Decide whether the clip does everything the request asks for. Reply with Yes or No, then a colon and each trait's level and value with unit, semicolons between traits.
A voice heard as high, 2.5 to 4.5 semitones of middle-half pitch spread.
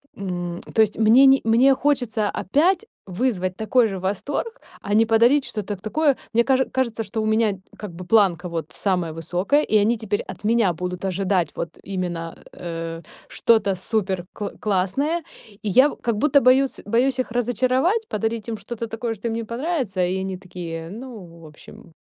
No: high, 215 Hz; average, 5.0 semitones